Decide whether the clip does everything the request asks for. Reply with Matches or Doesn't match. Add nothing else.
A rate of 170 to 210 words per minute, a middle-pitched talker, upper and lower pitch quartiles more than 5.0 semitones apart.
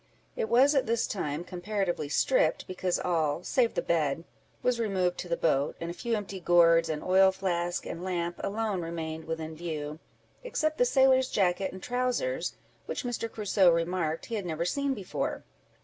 Matches